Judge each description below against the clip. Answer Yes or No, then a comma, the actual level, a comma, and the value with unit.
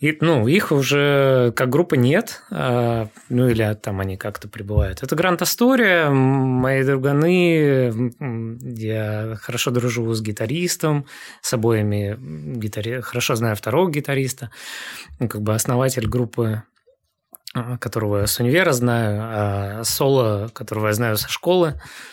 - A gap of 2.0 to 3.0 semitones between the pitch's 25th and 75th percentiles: No, average, 4.2 semitones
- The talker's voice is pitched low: Yes, low, 125 Hz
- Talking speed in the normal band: Yes, average, 125 wpm